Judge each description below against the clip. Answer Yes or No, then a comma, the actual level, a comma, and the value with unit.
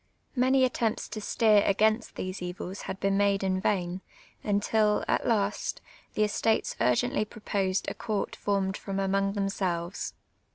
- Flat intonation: Yes, narrow, 1.9 semitones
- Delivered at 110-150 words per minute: Yes, average, 140 wpm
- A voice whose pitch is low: No, high, 200 Hz